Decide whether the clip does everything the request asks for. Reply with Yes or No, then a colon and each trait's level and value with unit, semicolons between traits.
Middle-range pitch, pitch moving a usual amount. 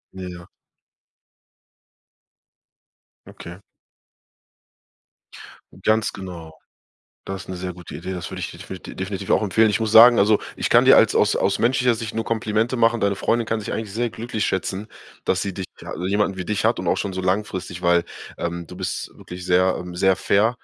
No: very low, 95 Hz; average, 3.3 semitones